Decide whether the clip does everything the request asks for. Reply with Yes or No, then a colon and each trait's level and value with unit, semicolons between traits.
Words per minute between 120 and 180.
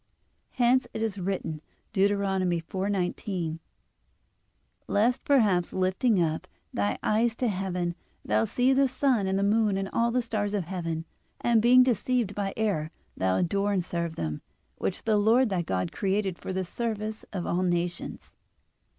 Yes: average, 155 wpm